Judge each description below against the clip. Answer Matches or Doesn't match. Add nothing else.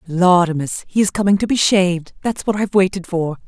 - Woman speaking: Matches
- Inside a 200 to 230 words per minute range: Matches